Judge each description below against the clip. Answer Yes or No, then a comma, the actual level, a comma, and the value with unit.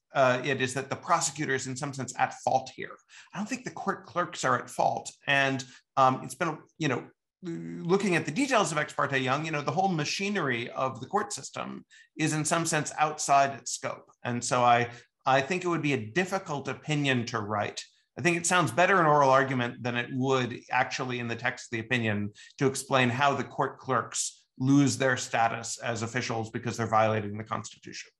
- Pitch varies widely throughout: No, average, 4.0 semitones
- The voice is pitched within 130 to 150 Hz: Yes, low, 135 Hz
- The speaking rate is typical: No, fast, 210 wpm